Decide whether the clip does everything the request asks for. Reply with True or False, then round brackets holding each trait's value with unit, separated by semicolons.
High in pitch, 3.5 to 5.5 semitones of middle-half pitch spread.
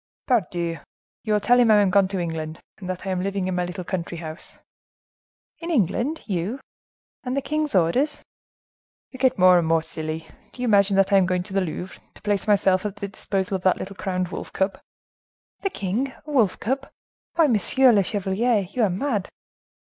True (195 Hz; 4.6 semitones)